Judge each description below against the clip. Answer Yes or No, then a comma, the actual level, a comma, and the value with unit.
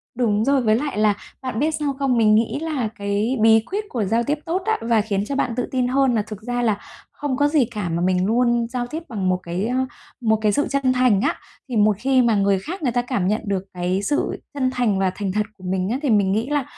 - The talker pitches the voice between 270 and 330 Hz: No, high, 230 Hz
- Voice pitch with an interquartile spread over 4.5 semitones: No, average, 4.2 semitones